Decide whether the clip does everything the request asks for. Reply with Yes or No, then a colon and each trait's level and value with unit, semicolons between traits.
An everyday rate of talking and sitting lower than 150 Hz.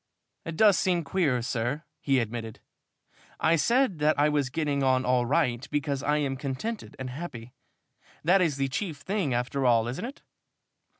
Yes: average, 170 wpm; medium, 140 Hz